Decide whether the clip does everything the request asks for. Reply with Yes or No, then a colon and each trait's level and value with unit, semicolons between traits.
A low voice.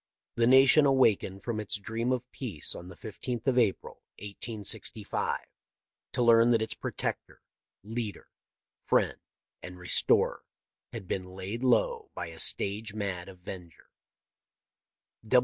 Yes: low, 110 Hz